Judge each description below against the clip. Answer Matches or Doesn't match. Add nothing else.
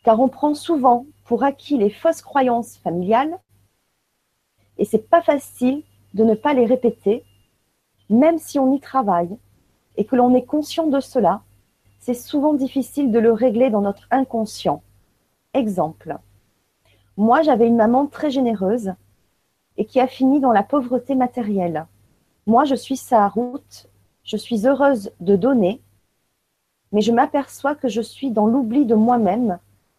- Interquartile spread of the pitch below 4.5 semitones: Doesn't match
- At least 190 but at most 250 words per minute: Doesn't match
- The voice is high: Matches